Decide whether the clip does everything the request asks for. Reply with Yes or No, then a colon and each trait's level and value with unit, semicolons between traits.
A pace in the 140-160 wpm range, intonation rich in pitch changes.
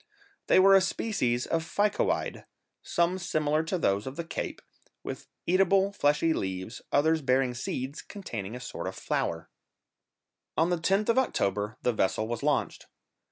Yes: average, 155 wpm; wide, 7.6 semitones